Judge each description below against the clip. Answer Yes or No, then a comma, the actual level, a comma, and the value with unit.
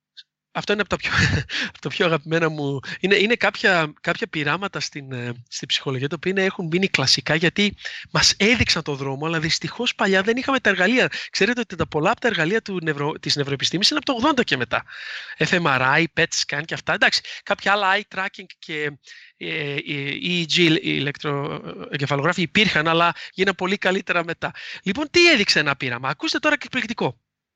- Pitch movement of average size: Yes, average, 5.0 semitones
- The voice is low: No, medium, 170 Hz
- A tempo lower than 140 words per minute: No, fast, 170 wpm